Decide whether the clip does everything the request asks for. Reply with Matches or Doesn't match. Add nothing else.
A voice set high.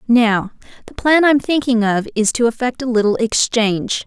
Matches